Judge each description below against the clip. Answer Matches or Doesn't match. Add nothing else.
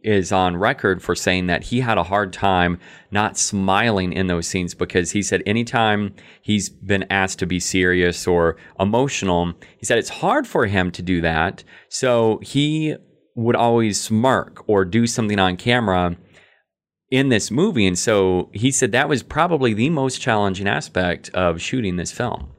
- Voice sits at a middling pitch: Doesn't match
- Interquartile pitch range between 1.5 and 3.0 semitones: Doesn't match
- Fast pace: Doesn't match